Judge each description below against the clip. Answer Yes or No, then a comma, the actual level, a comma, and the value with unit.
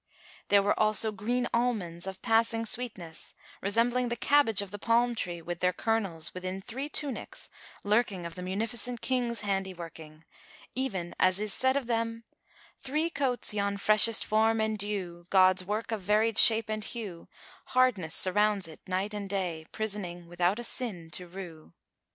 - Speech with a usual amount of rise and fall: Yes, average, 3.9 semitones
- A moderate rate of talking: Yes, average, 165 wpm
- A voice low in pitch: No, high, 210 Hz